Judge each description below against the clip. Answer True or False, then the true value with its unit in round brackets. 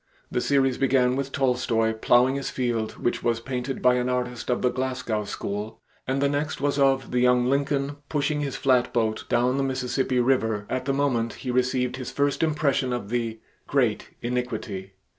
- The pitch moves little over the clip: True (2.0 semitones)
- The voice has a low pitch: True (125 Hz)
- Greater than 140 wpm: True (180 wpm)